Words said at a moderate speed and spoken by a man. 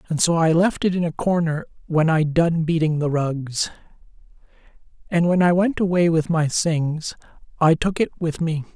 Yes: average, 185 wpm; male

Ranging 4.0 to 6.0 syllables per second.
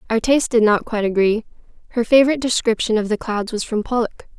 No: 7.0 syllables/s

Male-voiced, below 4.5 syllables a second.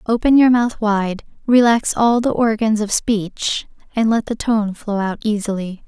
No: female; 4.2 syllables/s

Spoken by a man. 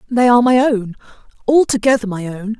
No: female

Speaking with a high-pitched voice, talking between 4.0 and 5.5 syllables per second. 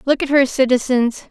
Yes: very high, 260 Hz; 5.2 syllables/s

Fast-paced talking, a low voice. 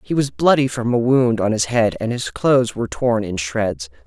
Yes: fast, 235 wpm; low, 115 Hz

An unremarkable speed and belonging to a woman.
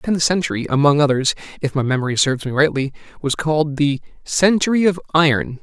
No: average, 180 wpm; male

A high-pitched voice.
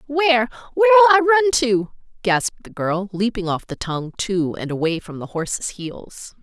Yes: high, 230 Hz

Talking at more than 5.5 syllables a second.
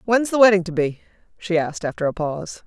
Yes: 6.5 syllables/s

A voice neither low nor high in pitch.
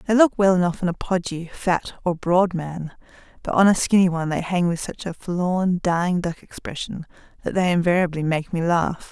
Yes: medium, 175 Hz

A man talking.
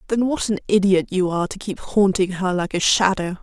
No: female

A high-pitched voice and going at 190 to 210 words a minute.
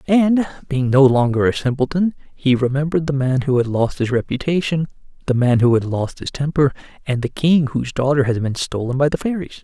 No: medium, 140 Hz; fast, 205 wpm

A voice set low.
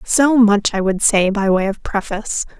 No: high, 210 Hz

